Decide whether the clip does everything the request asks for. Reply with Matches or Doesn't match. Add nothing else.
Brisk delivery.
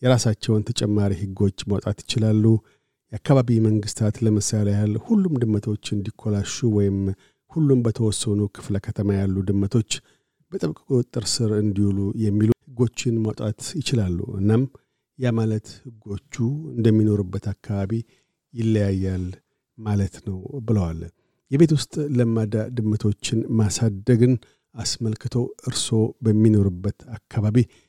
Doesn't match